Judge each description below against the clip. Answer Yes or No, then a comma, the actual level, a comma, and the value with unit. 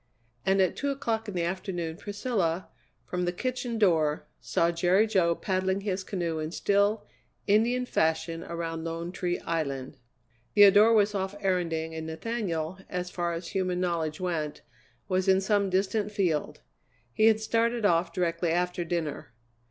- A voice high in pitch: No, medium, 180 Hz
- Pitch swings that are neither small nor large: Yes, average, 3.5 semitones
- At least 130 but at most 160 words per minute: Yes, average, 150 wpm